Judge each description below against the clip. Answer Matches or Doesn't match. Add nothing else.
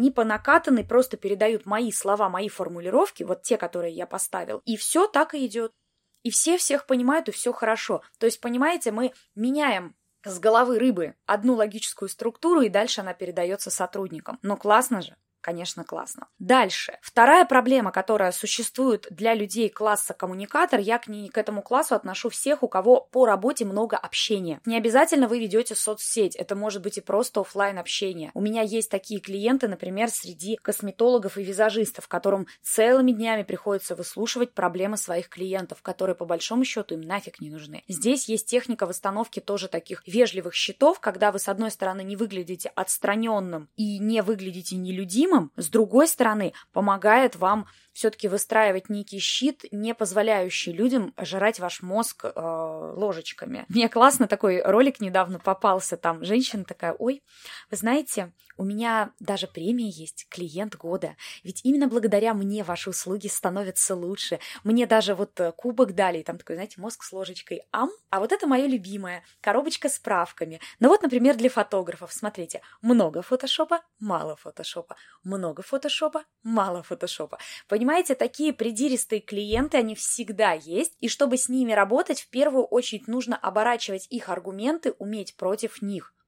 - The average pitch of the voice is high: Matches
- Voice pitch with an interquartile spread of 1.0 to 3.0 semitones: Doesn't match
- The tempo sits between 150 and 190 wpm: Matches